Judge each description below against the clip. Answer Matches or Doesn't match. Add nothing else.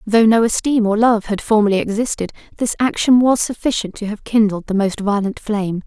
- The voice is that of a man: Doesn't match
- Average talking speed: Matches